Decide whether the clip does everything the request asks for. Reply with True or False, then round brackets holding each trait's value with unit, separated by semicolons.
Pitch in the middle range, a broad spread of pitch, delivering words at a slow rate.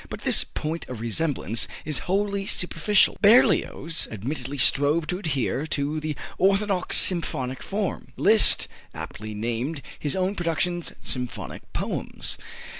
True (155 Hz; 5.9 semitones; 120 wpm)